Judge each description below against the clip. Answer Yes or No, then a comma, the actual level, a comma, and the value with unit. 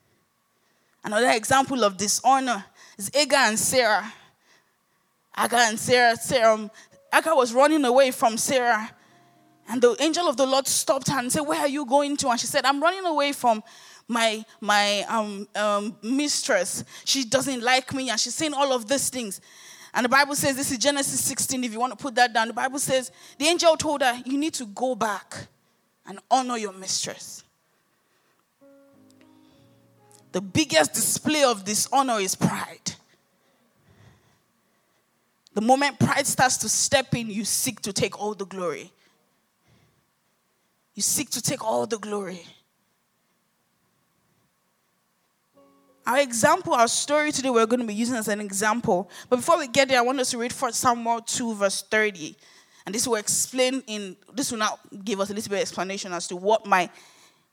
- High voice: Yes, high, 245 Hz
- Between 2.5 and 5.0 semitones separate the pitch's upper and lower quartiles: Yes, average, 4.6 semitones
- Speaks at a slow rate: No, average, 170 wpm